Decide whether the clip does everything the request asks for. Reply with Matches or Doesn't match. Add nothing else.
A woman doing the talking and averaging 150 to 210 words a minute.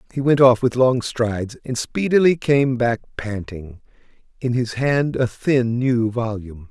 Doesn't match